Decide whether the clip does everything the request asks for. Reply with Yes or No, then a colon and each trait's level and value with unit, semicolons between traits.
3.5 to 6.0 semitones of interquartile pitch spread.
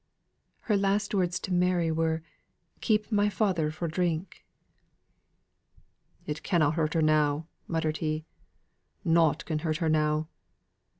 No: average, 2.8 semitones